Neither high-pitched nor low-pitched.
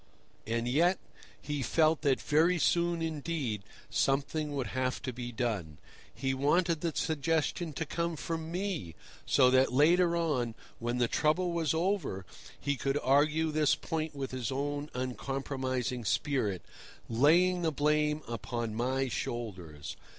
Yes: medium, 145 Hz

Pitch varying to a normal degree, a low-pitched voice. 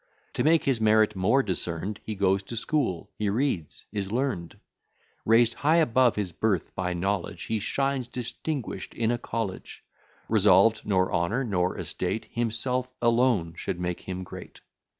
Yes: average, 4.6 semitones; low, 110 Hz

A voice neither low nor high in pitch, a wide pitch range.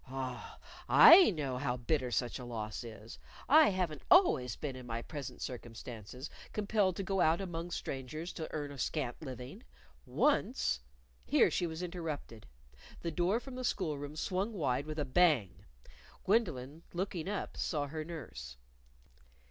Yes: medium, 150 Hz; wide, 6.1 semitones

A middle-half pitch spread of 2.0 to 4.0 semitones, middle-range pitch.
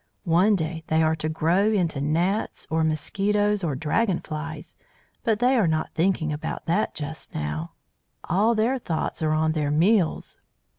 No: average, 4.6 semitones; medium, 165 Hz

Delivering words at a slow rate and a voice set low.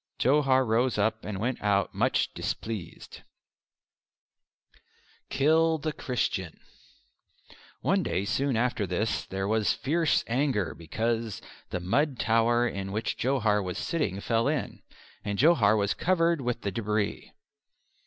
Yes: slow, 125 wpm; low, 115 Hz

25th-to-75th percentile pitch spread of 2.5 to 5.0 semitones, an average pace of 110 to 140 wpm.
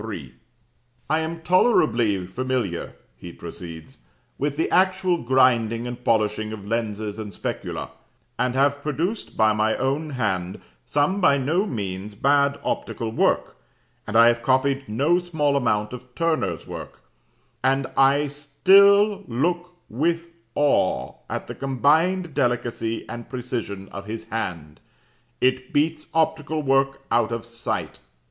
No: wide, 5.6 semitones; slow, 135 wpm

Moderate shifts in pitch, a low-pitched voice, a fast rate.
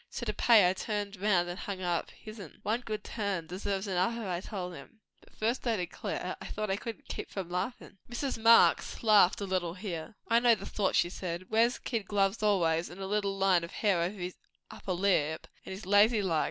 No: average, 3.1 semitones; high, 195 Hz; fast, 220 wpm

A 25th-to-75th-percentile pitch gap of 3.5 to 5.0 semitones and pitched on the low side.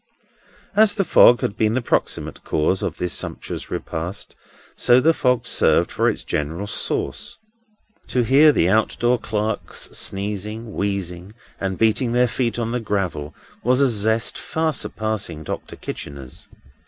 Yes: average, 4.2 semitones; low, 110 Hz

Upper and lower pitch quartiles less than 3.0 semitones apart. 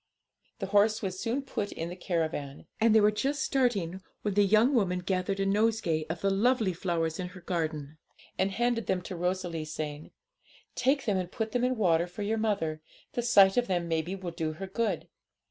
No: average, 4.4 semitones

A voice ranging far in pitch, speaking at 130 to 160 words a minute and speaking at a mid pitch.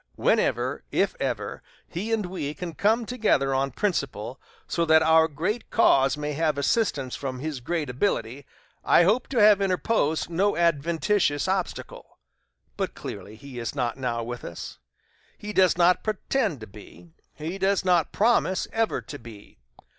Yes: wide, 6.5 semitones; average, 155 wpm; medium, 165 Hz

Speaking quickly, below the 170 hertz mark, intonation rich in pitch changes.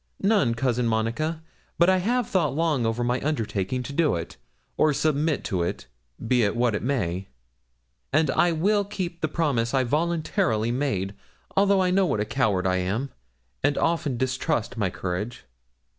No: average, 170 wpm; low, 135 Hz; wide, 6.5 semitones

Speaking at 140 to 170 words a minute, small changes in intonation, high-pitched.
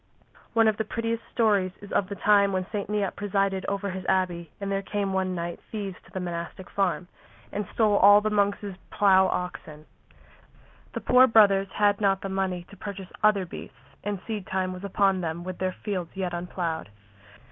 No: average, 190 wpm; narrow, 1.9 semitones; high, 195 Hz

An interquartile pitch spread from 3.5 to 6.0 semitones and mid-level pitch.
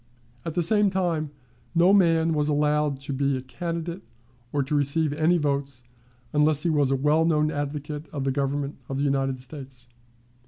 No: average, 2.7 semitones; medium, 150 Hz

